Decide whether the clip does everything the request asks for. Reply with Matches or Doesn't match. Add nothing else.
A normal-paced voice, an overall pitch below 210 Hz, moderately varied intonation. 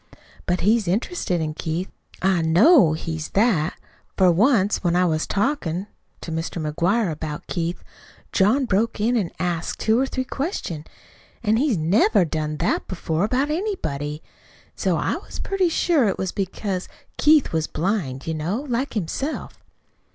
Doesn't match